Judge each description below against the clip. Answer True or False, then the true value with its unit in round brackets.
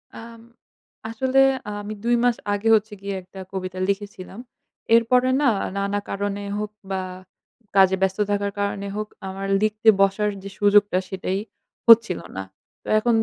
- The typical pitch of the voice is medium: False (205 Hz)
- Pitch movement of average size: False (2.0 semitones)